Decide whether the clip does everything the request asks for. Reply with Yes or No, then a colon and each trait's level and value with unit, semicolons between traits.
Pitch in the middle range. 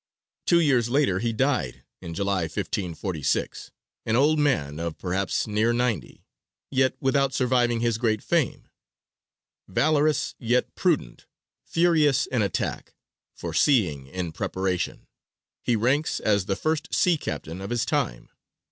No: low, 115 Hz